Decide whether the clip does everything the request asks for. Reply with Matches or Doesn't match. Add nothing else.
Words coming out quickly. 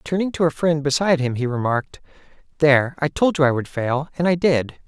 Matches